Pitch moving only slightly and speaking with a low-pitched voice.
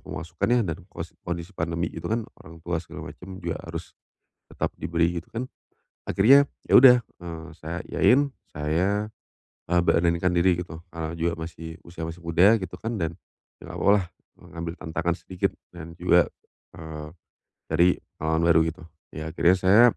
Yes: narrow, 2.2 semitones; very low, 85 Hz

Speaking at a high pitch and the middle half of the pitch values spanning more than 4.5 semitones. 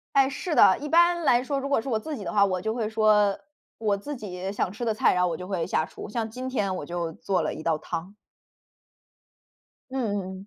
Yes: high, 210 Hz; wide, 5.5 semitones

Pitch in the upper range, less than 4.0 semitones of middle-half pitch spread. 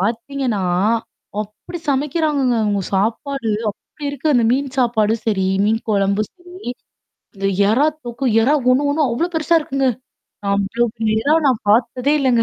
No: high, 245 Hz; average, 4.6 semitones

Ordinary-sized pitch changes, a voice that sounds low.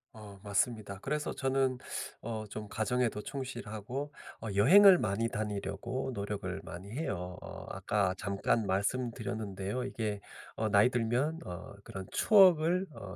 Yes: average, 4.5 semitones; low, 110 Hz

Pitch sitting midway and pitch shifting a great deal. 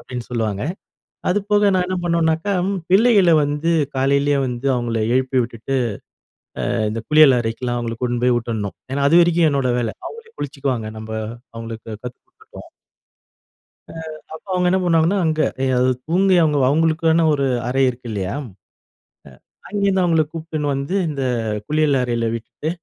Yes: medium, 145 Hz; wide, 5.7 semitones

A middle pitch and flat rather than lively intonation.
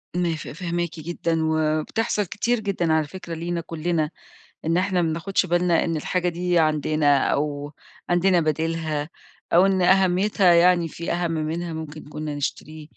Yes: medium, 170 Hz; narrow, 2.3 semitones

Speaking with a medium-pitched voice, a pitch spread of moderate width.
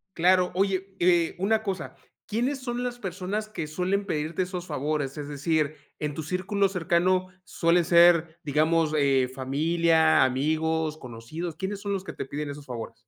Yes: medium, 170 Hz; average, 3.7 semitones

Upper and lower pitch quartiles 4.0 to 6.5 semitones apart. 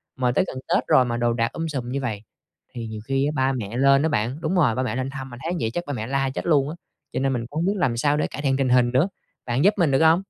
No: average, 3.5 semitones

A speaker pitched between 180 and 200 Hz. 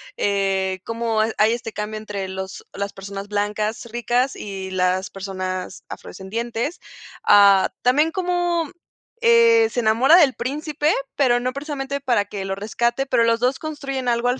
No: high, 230 Hz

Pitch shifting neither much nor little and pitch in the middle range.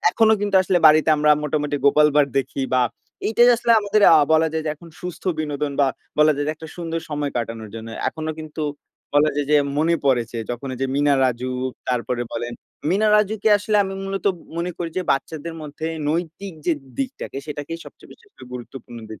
Yes: average, 4.4 semitones; medium, 150 Hz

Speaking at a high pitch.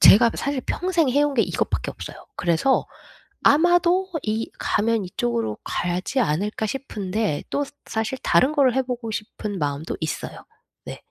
Yes: high, 225 Hz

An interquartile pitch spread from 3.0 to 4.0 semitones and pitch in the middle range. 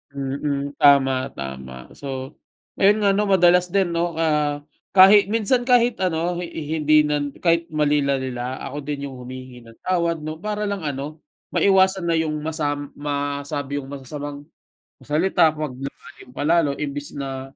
Yes: average, 3.7 semitones; medium, 150 Hz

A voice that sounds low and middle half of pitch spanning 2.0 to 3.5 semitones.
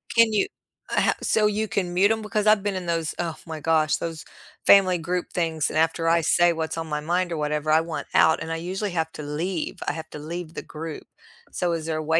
No: medium, 165 Hz; narrow, 2.5 semitones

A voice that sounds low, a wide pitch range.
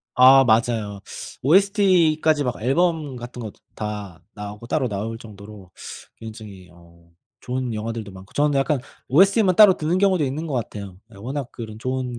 Yes: low, 120 Hz; wide, 6.1 semitones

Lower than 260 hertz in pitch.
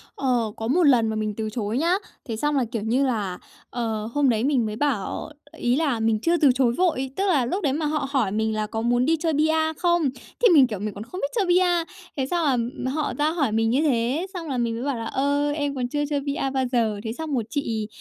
No: very high, 265 Hz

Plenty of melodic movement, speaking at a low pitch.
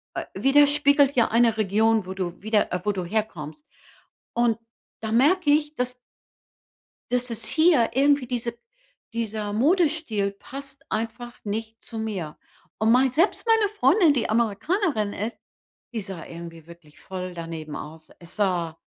No: wide, 5.9 semitones; high, 225 Hz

